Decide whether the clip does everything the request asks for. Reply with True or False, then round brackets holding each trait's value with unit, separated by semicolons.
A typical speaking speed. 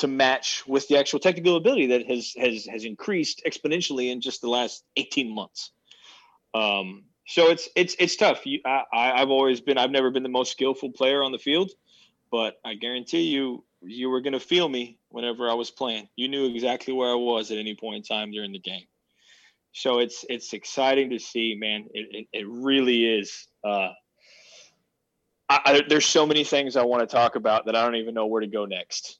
False (210 wpm)